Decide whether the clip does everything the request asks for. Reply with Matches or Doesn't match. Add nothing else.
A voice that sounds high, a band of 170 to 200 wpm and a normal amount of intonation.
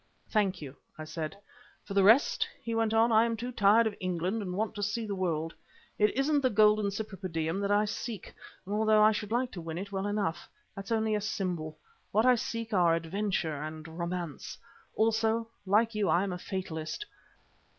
Matches